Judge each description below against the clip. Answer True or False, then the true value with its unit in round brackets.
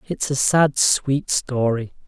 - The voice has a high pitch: False (135 Hz)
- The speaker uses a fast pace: False (145 wpm)